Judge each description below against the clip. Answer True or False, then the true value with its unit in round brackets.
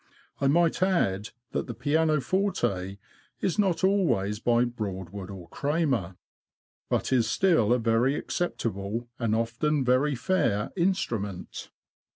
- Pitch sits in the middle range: False (120 Hz)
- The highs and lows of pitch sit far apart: True (7.7 semitones)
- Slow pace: True (125 wpm)